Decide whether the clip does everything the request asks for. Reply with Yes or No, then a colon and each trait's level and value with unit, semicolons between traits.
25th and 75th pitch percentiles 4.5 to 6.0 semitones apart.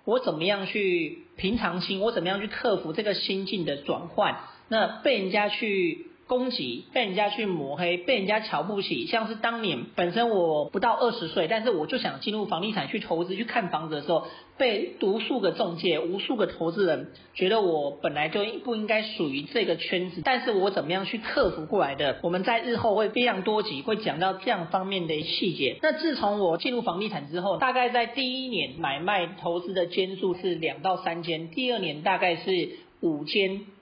Yes: average, 4.8 semitones